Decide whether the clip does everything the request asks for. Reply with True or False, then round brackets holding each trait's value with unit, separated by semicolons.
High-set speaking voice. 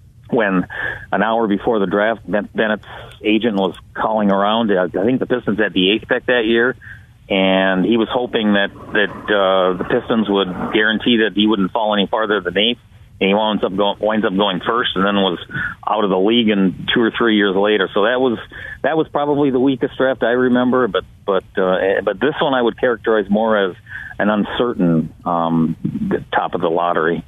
False (105 Hz)